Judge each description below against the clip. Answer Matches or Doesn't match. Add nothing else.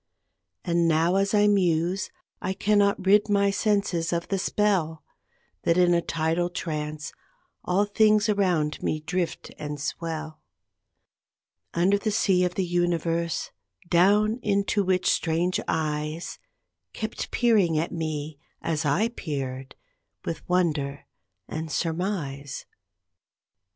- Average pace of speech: Doesn't match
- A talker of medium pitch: Matches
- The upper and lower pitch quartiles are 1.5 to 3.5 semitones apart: Doesn't match